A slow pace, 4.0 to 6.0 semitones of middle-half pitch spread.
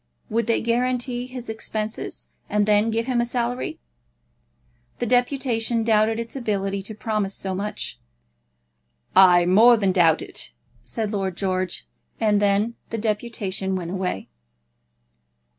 No: slow, 130 wpm; average, 3.3 semitones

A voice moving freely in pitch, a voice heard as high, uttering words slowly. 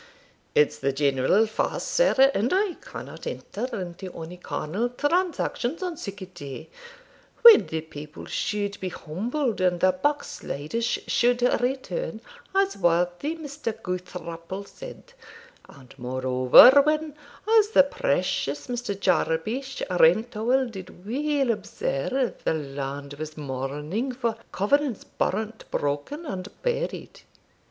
Yes: wide, 9.0 semitones; high, 205 Hz; slow, 120 wpm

